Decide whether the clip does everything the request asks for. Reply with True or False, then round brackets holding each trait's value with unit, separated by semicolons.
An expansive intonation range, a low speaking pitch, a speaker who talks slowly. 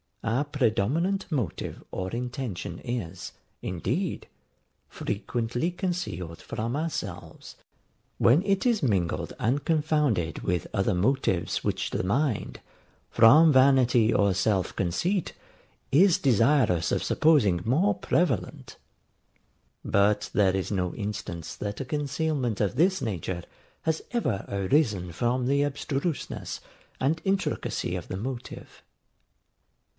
True (7.6 semitones; 120 Hz; 110 wpm)